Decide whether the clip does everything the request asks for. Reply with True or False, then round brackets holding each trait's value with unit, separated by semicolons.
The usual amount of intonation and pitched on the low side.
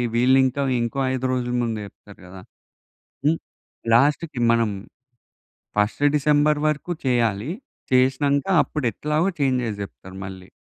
True (4.4 semitones; 130 Hz)